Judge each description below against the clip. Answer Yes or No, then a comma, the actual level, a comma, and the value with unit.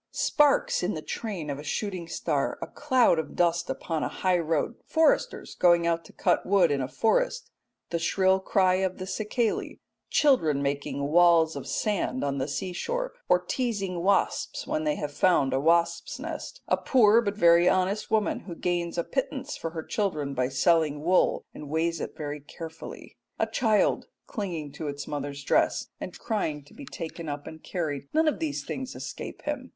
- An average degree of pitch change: No, wide, 5.8 semitones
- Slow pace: No, average, 185 wpm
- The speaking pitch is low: No, medium, 175 Hz